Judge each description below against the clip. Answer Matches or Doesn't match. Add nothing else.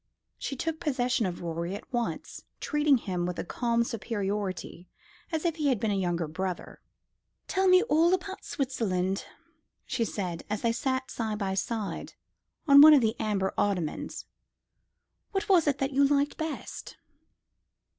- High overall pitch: Matches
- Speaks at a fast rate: Doesn't match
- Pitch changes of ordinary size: Doesn't match